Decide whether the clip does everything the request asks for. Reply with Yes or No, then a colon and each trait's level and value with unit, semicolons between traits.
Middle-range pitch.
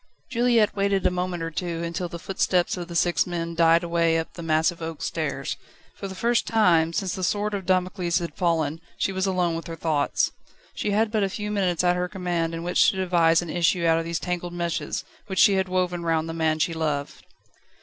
Yes: medium, 175 Hz